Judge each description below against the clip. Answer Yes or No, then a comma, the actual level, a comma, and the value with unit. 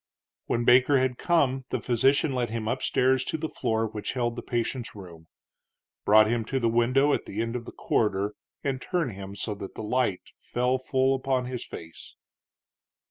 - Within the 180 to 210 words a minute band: Yes, average, 190 wpm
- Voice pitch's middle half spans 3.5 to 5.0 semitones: No, average, 3.0 semitones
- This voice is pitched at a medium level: No, low, 120 Hz